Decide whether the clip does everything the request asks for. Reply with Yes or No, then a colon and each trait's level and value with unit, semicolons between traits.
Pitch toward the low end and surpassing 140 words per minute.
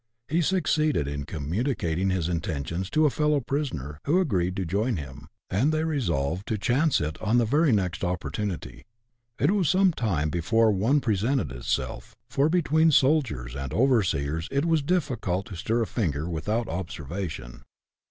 Yes: low, 105 Hz; average, 160 wpm